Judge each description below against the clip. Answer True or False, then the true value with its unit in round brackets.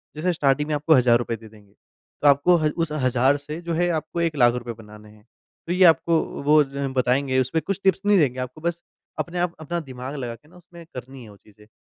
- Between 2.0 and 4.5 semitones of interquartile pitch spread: False (5.1 semitones)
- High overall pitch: False (145 Hz)